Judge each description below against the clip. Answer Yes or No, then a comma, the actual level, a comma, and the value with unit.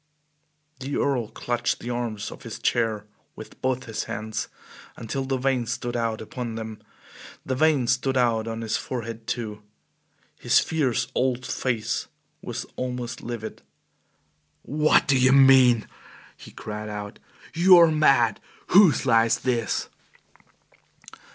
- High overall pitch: No, low, 120 Hz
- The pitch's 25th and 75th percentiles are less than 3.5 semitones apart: Yes, average, 2.8 semitones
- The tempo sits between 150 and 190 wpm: No, slow, 135 wpm